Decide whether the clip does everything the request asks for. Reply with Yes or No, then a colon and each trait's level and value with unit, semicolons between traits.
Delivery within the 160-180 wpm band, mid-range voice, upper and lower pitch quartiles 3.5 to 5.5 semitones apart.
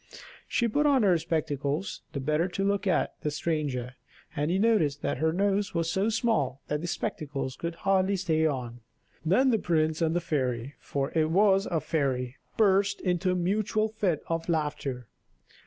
Yes: average, 175 wpm; medium, 165 Hz; average, 5.0 semitones